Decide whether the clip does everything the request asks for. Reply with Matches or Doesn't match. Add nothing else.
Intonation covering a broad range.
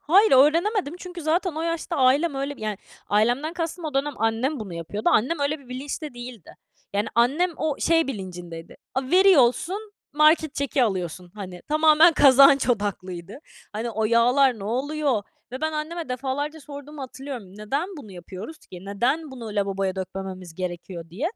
Matches